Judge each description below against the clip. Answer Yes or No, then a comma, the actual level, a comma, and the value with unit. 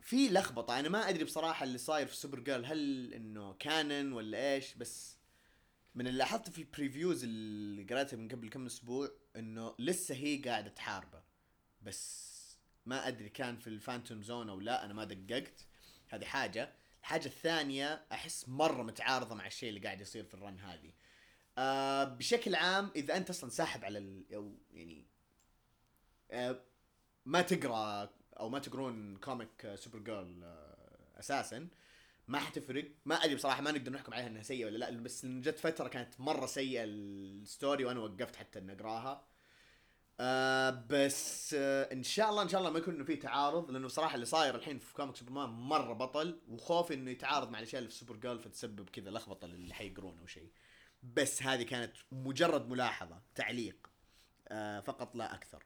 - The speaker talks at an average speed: No, fast, 165 wpm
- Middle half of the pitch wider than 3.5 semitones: Yes, average, 4.3 semitones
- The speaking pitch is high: No, low, 130 Hz